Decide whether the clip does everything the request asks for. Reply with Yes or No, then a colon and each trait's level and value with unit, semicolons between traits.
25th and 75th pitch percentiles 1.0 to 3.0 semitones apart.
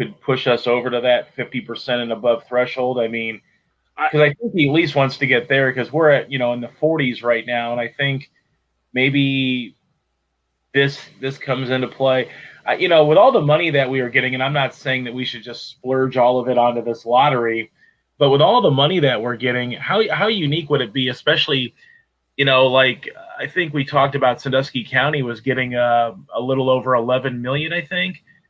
Yes: narrow, 2.6 semitones